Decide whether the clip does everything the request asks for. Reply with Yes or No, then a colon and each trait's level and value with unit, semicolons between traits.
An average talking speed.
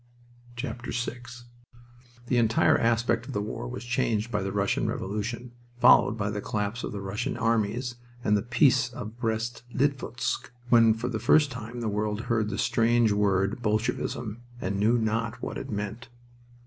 Yes: average, 160 wpm